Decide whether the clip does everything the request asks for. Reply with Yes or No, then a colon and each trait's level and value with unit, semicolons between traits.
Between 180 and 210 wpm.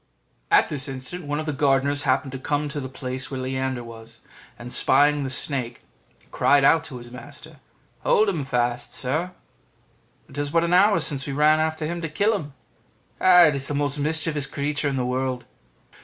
Yes: average, 190 wpm